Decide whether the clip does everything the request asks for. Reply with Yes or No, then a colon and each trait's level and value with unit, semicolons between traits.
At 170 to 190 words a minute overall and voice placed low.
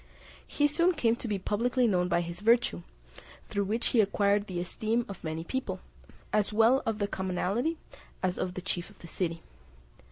No: average, 185 wpm; high, 205 Hz